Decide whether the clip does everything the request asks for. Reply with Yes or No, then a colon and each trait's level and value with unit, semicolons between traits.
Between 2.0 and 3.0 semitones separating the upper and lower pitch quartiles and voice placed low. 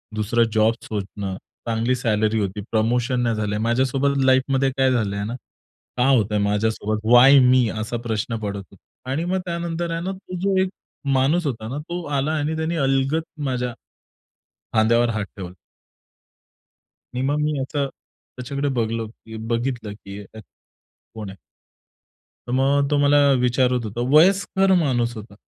No: average, 4.3 semitones; low, 125 Hz